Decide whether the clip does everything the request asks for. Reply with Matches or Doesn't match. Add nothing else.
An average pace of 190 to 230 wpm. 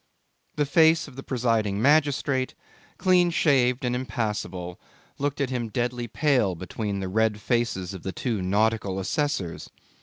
Doesn't match